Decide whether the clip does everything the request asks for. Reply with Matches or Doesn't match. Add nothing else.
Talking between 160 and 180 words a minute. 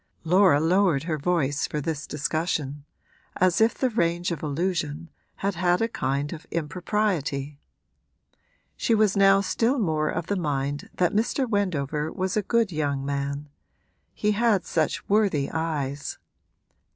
Doesn't match